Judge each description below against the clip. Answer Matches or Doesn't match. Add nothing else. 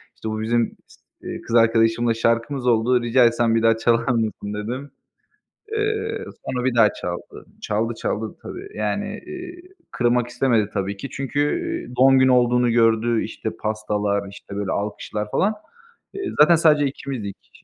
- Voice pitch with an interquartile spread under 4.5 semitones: Matches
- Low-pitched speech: Matches